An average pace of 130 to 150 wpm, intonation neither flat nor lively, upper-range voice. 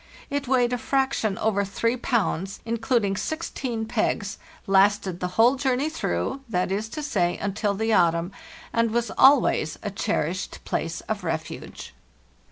Yes: average, 140 wpm; average, 4.3 semitones; high, 220 Hz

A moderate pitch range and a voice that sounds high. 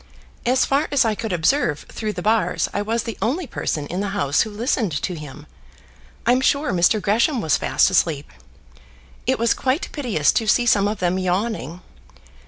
Yes: average, 5.0 semitones; high, 215 Hz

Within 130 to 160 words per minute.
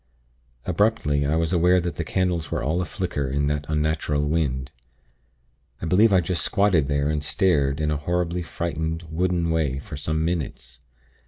No: average, 170 wpm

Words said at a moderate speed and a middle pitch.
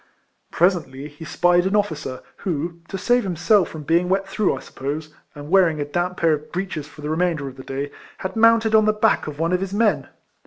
No: fast, 220 wpm; medium, 175 Hz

